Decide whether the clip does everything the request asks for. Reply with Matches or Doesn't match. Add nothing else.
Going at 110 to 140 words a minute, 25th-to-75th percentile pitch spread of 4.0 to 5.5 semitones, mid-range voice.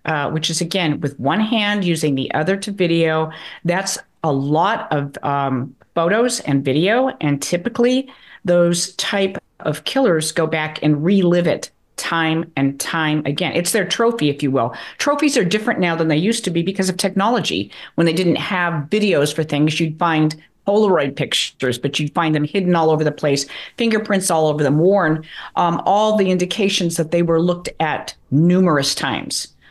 Doesn't match